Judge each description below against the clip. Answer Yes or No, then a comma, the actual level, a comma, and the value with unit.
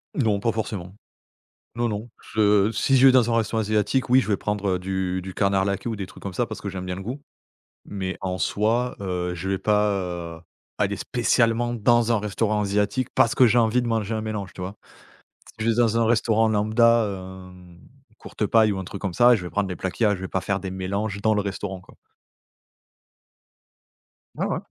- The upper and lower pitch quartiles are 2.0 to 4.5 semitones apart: Yes, average, 3.1 semitones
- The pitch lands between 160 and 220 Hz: No, low, 105 Hz